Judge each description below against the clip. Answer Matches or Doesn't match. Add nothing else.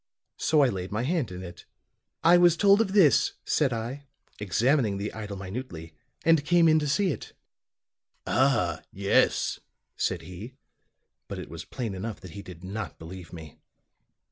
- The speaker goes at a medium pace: Matches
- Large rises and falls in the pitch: Matches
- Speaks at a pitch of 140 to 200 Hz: Doesn't match